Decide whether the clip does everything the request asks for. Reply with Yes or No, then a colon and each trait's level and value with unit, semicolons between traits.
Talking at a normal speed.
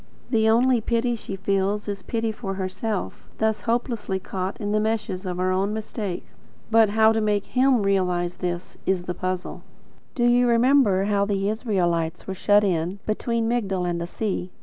Yes: average, 175 wpm